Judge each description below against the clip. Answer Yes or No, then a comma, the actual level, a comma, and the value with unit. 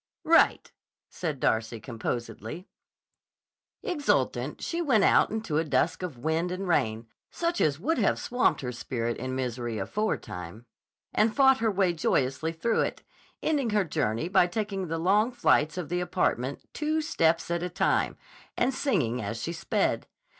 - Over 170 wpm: No, average, 155 wpm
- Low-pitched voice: No, medium, 170 Hz